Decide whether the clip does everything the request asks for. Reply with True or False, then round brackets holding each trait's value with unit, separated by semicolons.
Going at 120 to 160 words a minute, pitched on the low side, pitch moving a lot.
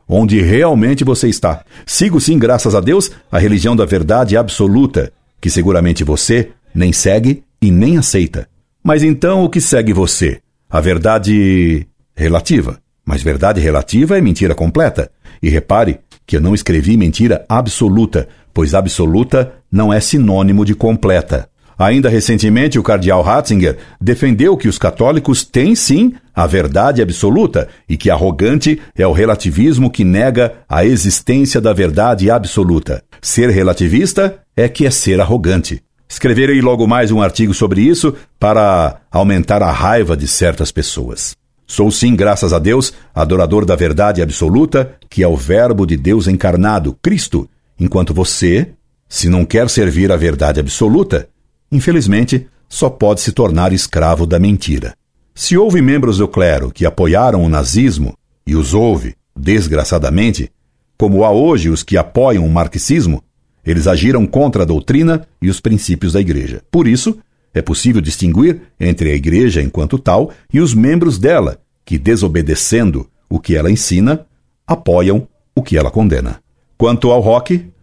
True (150 wpm; 100 Hz; 5.8 semitones)